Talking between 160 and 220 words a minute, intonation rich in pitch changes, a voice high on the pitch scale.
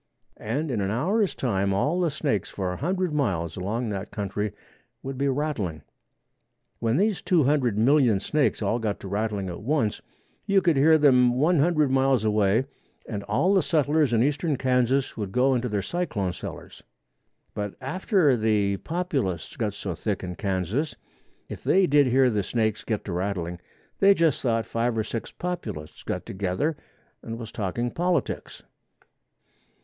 No: average, 165 wpm; wide, 6.5 semitones; low, 120 Hz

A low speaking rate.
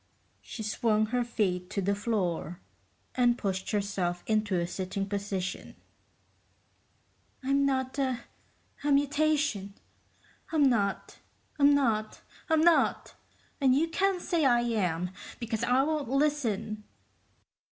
Yes: slow, 120 wpm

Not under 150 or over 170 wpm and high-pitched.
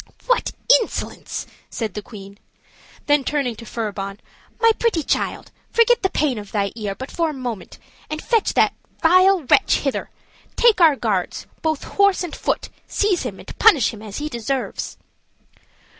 Yes: average, 160 wpm; very high, 275 Hz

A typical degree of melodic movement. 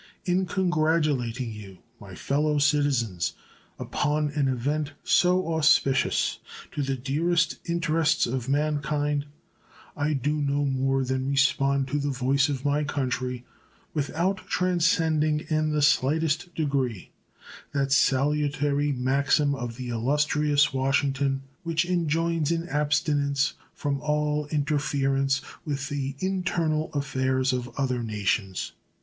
No: narrow, 2.3 semitones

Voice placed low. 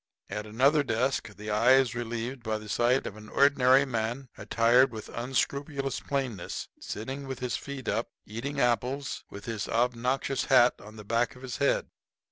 Yes: low, 125 Hz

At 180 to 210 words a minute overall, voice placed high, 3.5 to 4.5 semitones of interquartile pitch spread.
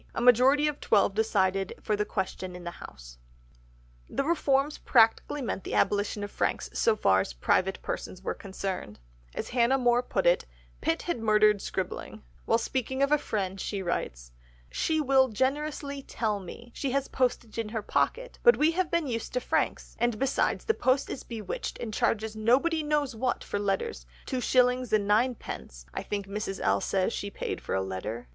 No: average, 185 wpm; high, 225 Hz; wide, 5.4 semitones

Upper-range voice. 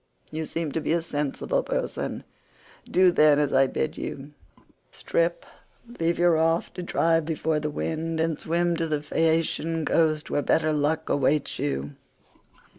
No: medium, 160 Hz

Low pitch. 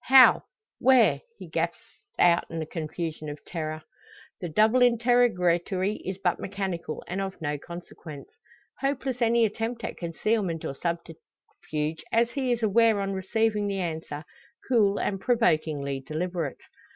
No: high, 190 Hz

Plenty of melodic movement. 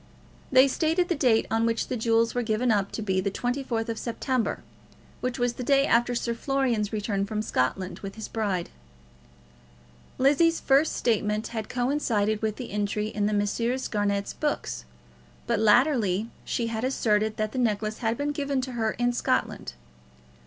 No: average, 3.1 semitones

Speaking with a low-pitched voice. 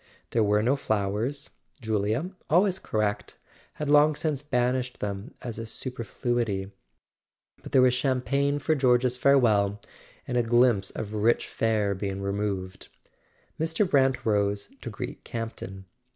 Yes: low, 120 Hz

